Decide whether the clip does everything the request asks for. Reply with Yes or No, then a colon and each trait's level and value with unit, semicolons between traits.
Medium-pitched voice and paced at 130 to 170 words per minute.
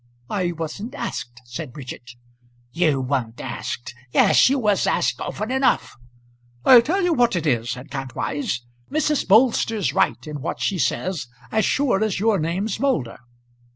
Yes: medium, 180 Hz; average, 155 wpm